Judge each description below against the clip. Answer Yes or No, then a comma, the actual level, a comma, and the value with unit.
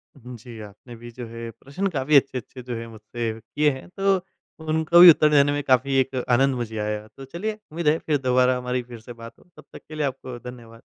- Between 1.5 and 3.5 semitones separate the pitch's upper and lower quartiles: No, average, 3.9 semitones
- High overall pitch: No, low, 130 Hz